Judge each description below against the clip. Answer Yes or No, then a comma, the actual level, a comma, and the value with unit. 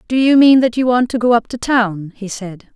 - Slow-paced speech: No, fast, 285 wpm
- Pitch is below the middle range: No, high, 230 Hz